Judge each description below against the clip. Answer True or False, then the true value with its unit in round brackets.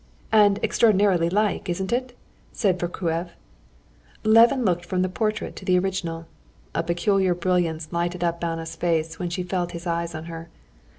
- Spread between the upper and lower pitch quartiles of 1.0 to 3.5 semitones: True (2.4 semitones)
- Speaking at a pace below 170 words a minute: True (160 wpm)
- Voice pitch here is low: False (175 Hz)